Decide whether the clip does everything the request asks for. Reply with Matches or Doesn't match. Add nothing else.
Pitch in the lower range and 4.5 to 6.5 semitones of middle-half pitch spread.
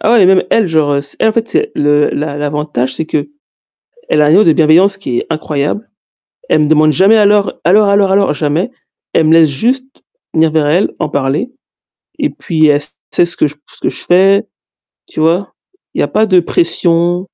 Doesn't match